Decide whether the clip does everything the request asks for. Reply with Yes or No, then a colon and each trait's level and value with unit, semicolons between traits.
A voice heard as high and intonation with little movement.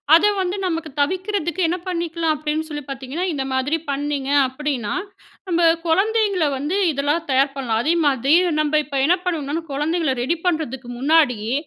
No: very high, 300 Hz; average, 3.7 semitones